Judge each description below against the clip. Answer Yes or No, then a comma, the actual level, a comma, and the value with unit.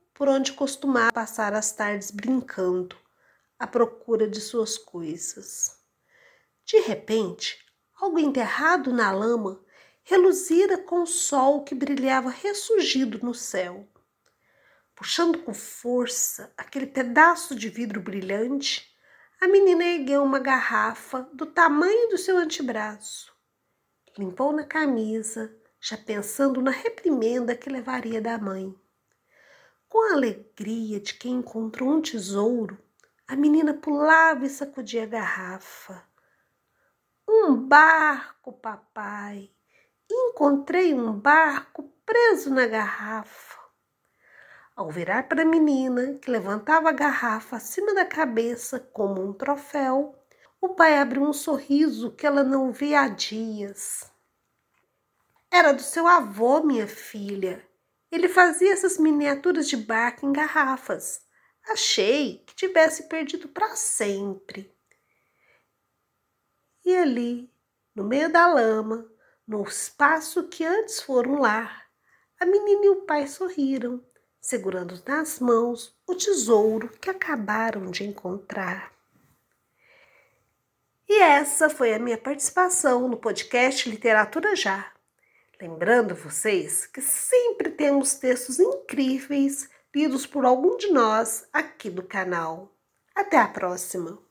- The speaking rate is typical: No, slow, 115 wpm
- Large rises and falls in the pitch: Yes, wide, 6.3 semitones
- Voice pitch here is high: Yes, very high, 270 Hz